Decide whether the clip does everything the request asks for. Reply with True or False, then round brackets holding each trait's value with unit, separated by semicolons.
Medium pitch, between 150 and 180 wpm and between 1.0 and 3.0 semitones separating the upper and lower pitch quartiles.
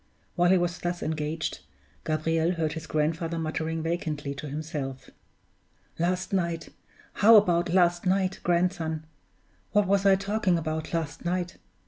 False (170 Hz; 135 wpm; 2.4 semitones)